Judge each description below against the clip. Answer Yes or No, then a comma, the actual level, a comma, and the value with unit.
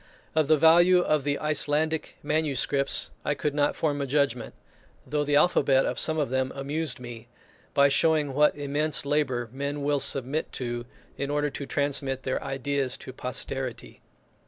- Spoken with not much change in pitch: Yes, narrow, 2.0 semitones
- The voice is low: No, medium, 145 Hz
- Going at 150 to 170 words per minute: Yes, average, 160 wpm